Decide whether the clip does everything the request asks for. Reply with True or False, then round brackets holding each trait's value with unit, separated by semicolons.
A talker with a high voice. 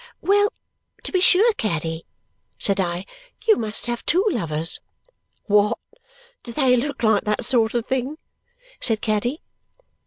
True (235 Hz)